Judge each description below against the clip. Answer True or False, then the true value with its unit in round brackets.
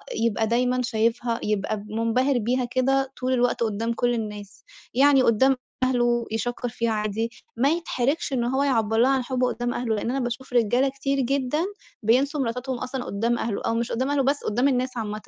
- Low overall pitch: False (245 Hz)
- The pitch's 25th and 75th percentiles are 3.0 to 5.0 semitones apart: False (2.4 semitones)